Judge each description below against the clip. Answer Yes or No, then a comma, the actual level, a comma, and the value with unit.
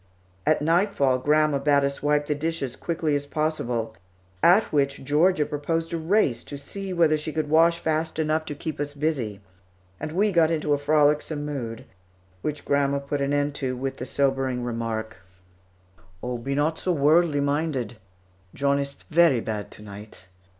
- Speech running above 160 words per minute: Yes, average, 170 wpm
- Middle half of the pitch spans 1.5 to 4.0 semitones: Yes, average, 2.7 semitones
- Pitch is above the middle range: No, medium, 145 Hz